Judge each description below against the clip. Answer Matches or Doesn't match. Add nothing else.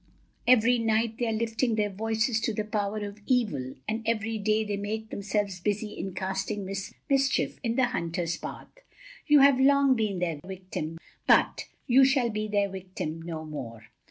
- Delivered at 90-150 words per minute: Doesn't match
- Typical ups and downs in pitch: Matches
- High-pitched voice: Matches